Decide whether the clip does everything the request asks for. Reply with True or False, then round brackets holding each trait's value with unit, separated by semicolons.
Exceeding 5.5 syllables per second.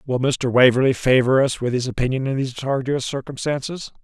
True (5.9 syllables/s)